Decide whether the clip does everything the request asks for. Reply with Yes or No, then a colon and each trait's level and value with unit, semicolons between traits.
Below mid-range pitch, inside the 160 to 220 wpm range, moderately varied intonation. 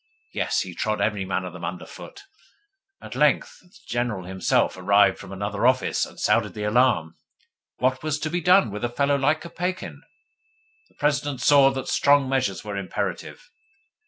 No: low, 120 Hz; average, 170 wpm; wide, 6.6 semitones